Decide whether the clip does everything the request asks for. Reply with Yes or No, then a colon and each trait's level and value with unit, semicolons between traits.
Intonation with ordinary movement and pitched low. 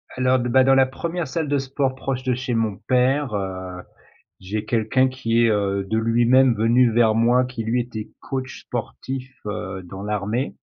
Yes: average, 3.3 semitones; low, 120 Hz